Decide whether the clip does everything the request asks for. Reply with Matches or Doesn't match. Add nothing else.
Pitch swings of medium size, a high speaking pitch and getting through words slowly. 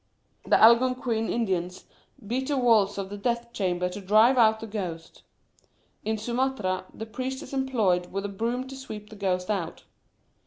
Doesn't match